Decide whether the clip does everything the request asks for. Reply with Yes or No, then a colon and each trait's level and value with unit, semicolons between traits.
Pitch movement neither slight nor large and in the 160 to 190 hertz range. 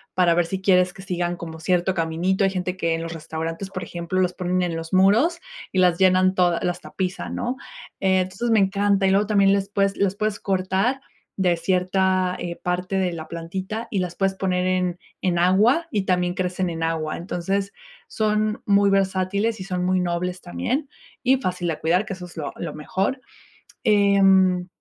No: narrow, 1.8 semitones; medium, 185 Hz